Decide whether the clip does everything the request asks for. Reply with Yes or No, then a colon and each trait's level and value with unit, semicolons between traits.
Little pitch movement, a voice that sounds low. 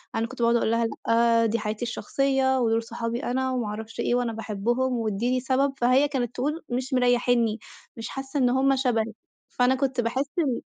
No: narrow, 2.3 semitones; high, 245 Hz